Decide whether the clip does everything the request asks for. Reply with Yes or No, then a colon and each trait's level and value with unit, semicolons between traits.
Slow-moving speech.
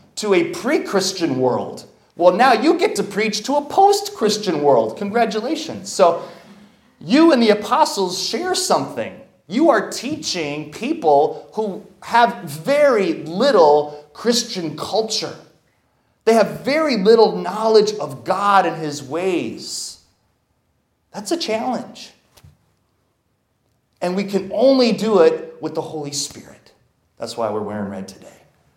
Yes: slow, 130 wpm